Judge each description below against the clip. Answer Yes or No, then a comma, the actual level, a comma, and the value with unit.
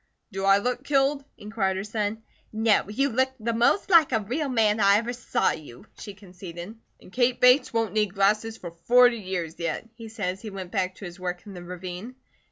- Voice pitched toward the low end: No, high, 210 Hz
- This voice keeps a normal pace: No, fast, 210 wpm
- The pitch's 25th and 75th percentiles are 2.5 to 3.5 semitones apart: No, average, 4.0 semitones